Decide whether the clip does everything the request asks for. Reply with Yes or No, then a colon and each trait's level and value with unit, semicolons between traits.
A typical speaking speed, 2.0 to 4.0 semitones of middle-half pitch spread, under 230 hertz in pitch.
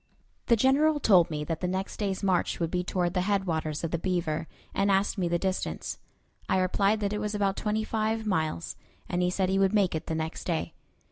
No: fast, 220 wpm; average, 3.3 semitones; high, 190 Hz